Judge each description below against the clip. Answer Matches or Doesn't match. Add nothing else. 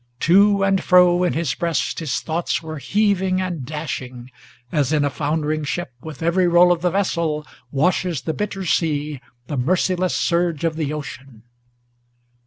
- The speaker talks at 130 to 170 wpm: Matches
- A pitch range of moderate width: Matches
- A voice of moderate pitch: Matches